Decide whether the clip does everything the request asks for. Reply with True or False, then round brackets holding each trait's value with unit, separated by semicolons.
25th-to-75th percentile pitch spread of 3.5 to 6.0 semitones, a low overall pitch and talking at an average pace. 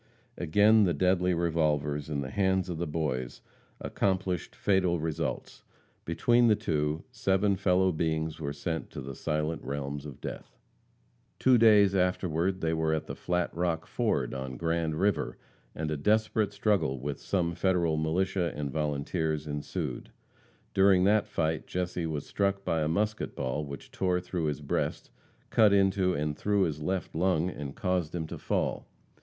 True (3.8 semitones; 85 Hz; 160 wpm)